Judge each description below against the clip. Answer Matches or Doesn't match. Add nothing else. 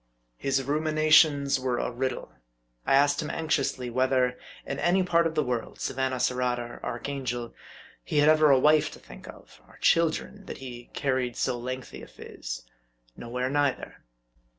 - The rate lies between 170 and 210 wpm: Doesn't match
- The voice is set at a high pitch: Doesn't match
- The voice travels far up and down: Doesn't match